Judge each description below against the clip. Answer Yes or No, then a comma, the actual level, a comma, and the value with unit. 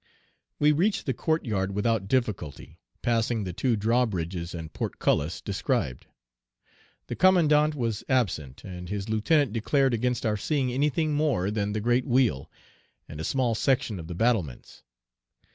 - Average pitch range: No, wide, 5.7 semitones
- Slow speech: No, average, 145 wpm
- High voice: No, low, 115 Hz